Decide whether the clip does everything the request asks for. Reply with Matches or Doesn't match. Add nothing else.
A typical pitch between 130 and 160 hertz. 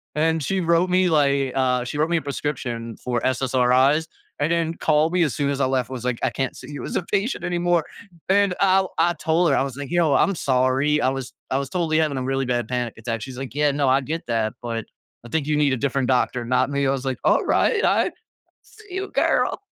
Matches